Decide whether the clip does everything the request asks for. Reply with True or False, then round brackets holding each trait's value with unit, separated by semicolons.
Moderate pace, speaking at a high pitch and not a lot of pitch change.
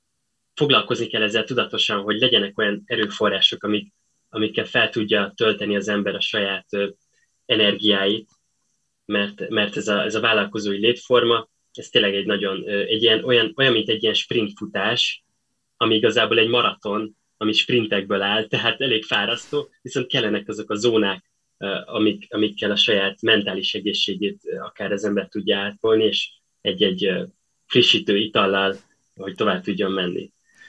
False (145 wpm; 105 Hz; 1.7 semitones)